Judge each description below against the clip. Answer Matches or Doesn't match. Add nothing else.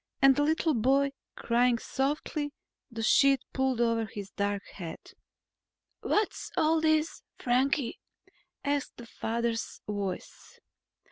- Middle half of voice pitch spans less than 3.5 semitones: Doesn't match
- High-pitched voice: Matches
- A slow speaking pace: Matches